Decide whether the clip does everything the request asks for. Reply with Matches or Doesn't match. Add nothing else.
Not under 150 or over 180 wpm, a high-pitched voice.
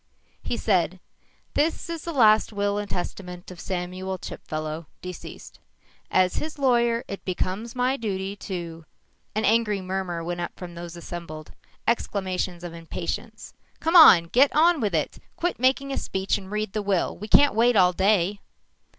Matches